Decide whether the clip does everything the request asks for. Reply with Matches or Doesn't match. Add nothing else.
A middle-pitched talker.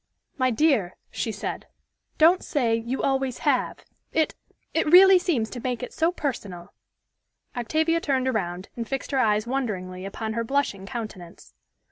Doesn't match